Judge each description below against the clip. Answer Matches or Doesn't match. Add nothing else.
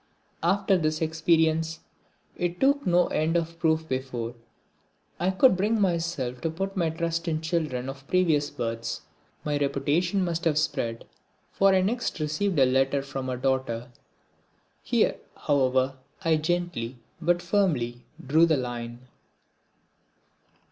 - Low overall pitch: Doesn't match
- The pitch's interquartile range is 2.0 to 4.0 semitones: Doesn't match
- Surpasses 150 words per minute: Doesn't match